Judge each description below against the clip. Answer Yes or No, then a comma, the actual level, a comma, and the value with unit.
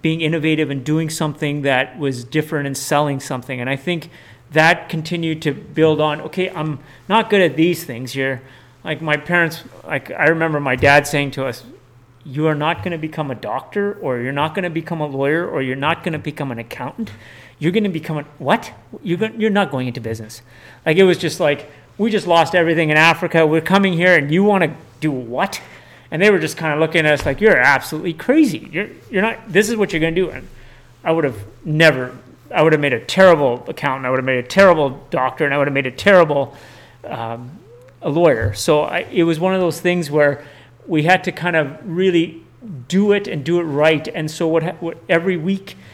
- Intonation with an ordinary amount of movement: Yes, average, 4.1 semitones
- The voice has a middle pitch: Yes, medium, 155 Hz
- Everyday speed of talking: No, fast, 225 wpm